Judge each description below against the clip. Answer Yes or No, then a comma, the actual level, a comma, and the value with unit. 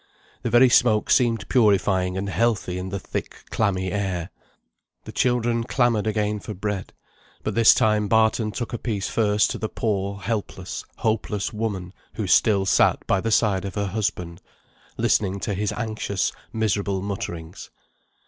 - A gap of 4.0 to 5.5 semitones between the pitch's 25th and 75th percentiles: No, narrow, 2.6 semitones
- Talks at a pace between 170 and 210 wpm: No, average, 155 wpm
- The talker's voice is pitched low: Yes, low, 105 Hz